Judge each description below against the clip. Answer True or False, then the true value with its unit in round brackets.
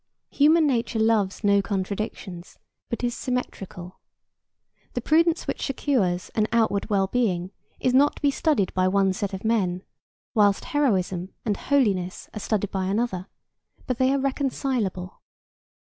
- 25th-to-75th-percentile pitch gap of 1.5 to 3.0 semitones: False (5.2 semitones)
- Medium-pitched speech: False (215 Hz)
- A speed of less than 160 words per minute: True (145 wpm)